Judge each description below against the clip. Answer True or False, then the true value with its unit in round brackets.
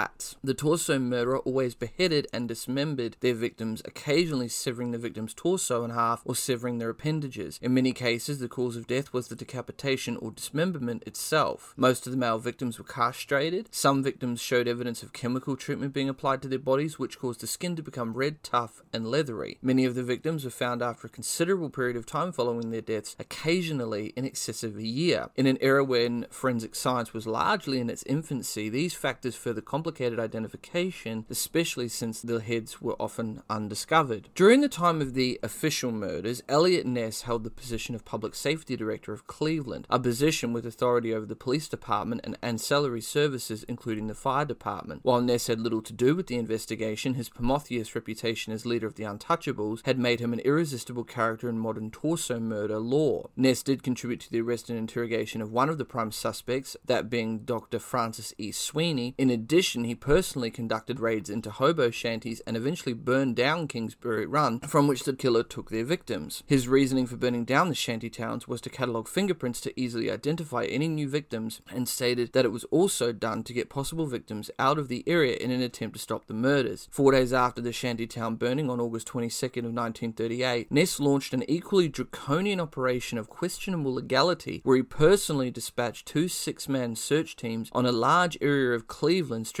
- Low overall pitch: True (125 Hz)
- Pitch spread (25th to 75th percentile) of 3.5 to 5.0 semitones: False (2.9 semitones)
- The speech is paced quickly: False (190 wpm)